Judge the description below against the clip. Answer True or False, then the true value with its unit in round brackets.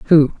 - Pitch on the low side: False (150 Hz)